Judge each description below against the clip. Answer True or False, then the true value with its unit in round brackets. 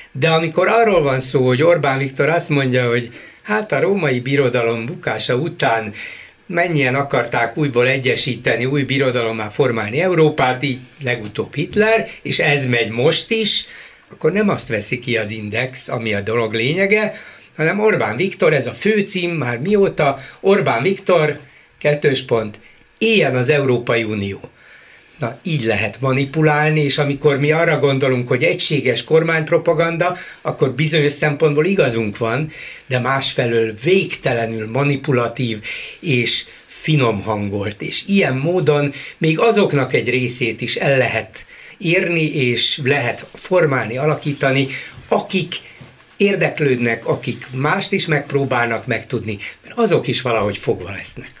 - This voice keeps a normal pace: True (130 wpm)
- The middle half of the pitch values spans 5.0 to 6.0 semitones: True (5.3 semitones)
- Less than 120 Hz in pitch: False (140 Hz)